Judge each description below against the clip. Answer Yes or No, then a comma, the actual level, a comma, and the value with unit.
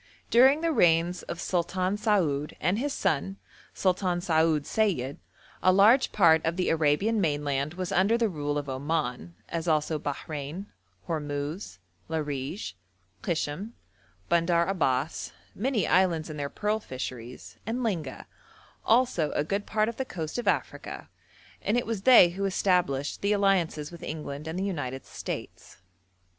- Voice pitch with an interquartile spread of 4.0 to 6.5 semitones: Yes, average, 5.3 semitones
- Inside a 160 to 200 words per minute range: No, average, 145 wpm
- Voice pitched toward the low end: No, medium, 170 Hz